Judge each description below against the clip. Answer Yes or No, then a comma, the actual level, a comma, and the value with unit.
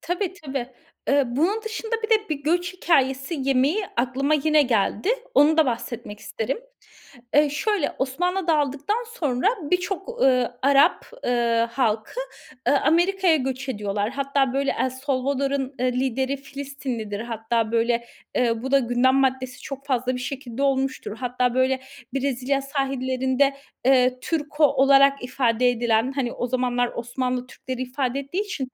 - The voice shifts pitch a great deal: No, narrow, 2.4 semitones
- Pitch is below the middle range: No, very high, 265 Hz